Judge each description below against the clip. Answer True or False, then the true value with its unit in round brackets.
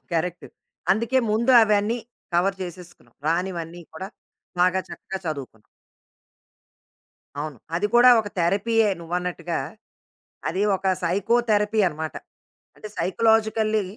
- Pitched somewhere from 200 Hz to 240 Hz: False (190 Hz)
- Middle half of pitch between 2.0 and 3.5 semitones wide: False (4.1 semitones)